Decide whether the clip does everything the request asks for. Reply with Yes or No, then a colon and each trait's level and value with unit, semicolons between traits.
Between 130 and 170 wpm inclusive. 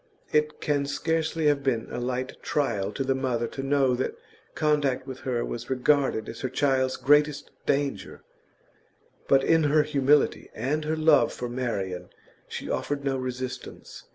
Yes: average, 155 wpm